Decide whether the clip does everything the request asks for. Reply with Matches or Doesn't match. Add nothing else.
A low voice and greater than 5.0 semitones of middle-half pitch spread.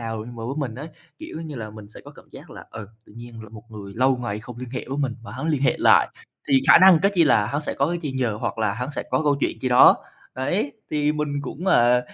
Doesn't match